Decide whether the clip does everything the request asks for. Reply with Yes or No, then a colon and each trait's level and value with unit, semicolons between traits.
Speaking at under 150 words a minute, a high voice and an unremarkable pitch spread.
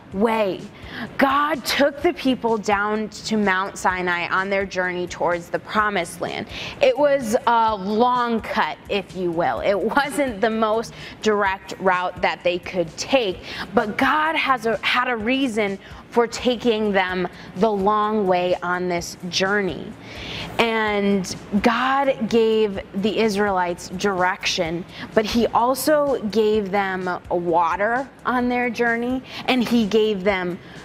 Yes: slow, 135 wpm; high, 210 Hz; average, 4.4 semitones